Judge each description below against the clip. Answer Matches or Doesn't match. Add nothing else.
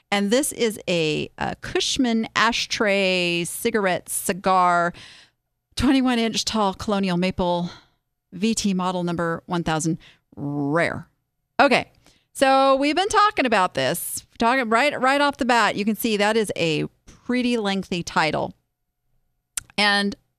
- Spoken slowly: Matches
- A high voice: Matches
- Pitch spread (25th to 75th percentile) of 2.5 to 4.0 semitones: Doesn't match